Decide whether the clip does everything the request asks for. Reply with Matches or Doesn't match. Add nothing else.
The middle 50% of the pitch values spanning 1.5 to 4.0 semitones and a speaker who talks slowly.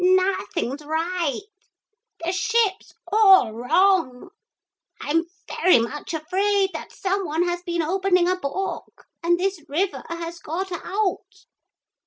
Matches